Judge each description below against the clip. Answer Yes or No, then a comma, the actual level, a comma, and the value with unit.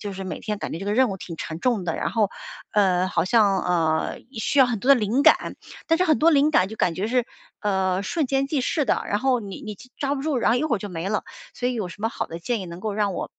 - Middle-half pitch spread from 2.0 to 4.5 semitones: No, average, 5.3 semitones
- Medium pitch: No, high, 210 Hz